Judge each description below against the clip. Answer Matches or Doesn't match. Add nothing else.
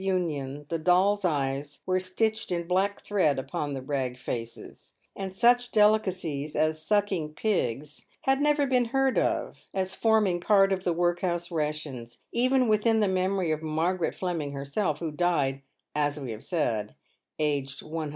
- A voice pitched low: Doesn't match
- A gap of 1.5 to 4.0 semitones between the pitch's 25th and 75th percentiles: Doesn't match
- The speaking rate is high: Doesn't match